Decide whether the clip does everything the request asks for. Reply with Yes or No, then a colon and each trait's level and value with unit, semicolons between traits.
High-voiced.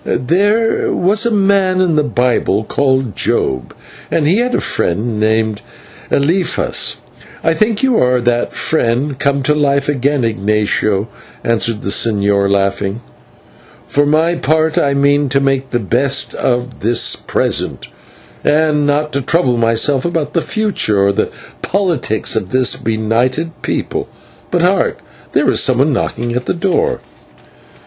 No: low, 135 Hz